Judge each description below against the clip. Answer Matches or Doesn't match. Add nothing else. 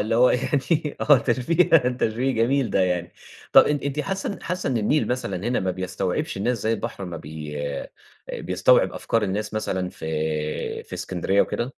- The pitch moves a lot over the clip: Matches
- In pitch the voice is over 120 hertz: Doesn't match